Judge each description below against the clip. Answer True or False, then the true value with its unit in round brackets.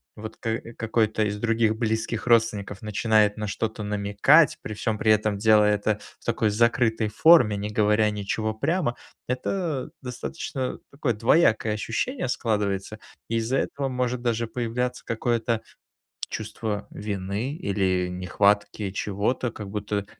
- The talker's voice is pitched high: False (110 Hz)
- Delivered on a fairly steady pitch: True (2.3 semitones)